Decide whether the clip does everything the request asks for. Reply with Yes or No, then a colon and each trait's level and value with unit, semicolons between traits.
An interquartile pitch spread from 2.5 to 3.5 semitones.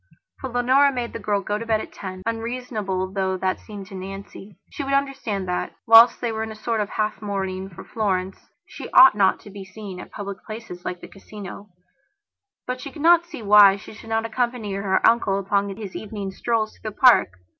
Yes: average, 3.1 semitones